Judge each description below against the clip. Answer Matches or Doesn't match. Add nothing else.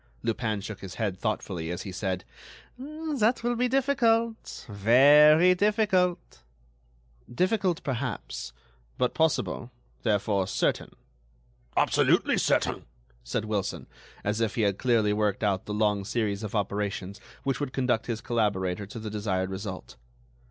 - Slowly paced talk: Matches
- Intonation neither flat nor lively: Doesn't match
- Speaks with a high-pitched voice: Doesn't match